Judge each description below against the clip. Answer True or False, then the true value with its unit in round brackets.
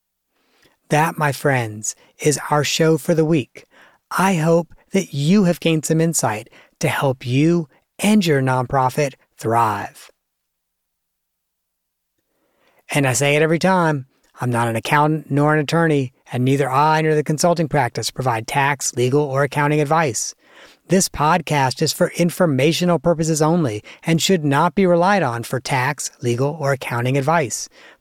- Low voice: False (145 Hz)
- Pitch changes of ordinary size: True (4.5 semitones)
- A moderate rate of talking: True (150 wpm)